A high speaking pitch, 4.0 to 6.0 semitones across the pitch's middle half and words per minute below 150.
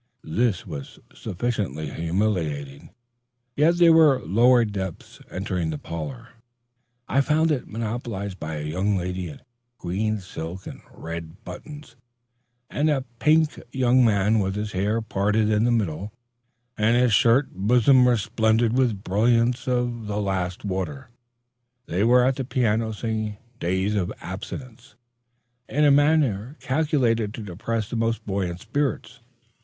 No: low, 110 Hz; average, 4.7 semitones; average, 140 wpm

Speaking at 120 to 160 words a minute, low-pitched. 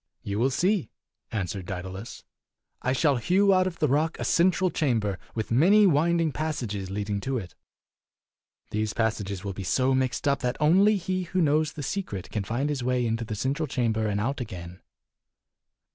No: average, 180 wpm; low, 130 Hz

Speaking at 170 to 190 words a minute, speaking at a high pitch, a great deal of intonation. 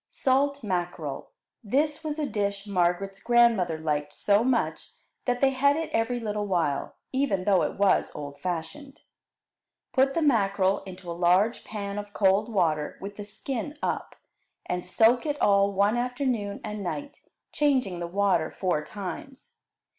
No: average, 155 wpm; high, 205 Hz; wide, 5.9 semitones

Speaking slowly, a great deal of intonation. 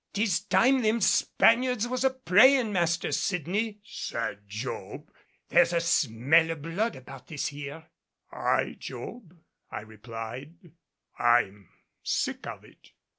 Yes: slow, 125 wpm; wide, 9.0 semitones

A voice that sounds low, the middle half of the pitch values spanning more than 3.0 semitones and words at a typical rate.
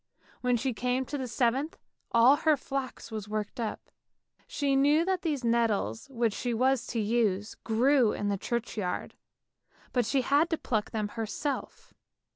No: high, 240 Hz; average, 3.7 semitones; average, 160 wpm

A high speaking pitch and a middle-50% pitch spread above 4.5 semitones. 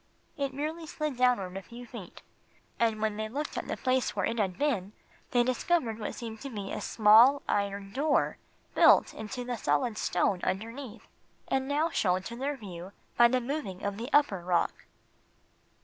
Yes: high, 235 Hz; average, 5.0 semitones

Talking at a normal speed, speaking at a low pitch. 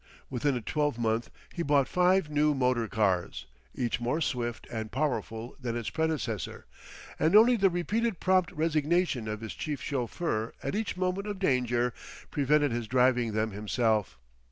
Yes: average, 155 wpm; low, 130 Hz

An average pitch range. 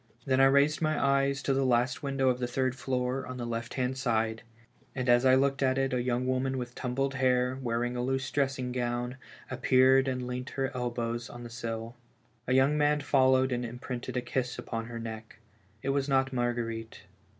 No: narrow, 1.7 semitones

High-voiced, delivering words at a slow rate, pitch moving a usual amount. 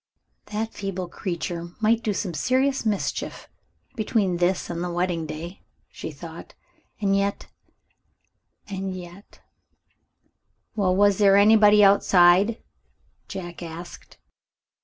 Yes: high, 195 Hz; slow, 115 wpm; average, 3.1 semitones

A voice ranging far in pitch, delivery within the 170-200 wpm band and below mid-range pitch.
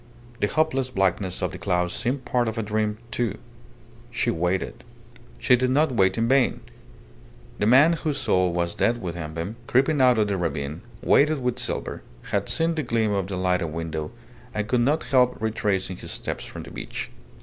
Yes: wide, 5.7 semitones; average, 185 wpm; low, 110 Hz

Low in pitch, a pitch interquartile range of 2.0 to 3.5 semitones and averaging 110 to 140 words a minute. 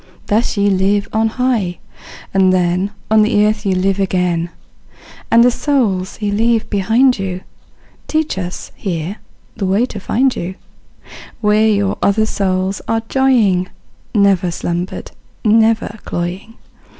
No: high, 200 Hz; average, 3.2 semitones; slow, 135 wpm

